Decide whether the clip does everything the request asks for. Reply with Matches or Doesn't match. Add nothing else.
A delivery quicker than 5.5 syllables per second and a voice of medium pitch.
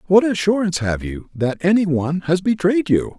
Doesn't match